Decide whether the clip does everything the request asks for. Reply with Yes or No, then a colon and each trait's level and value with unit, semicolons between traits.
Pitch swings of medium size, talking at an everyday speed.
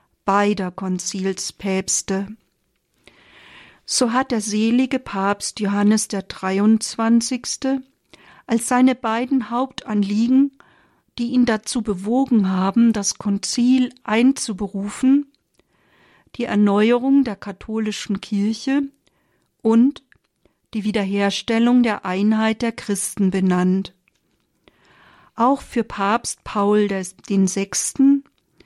No: average, 3.7 semitones; slow, 85 wpm